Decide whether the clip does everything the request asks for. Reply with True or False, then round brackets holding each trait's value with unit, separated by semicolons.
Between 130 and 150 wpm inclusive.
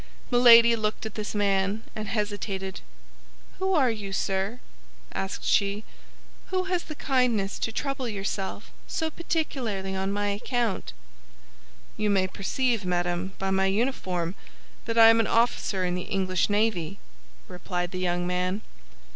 True (140 wpm)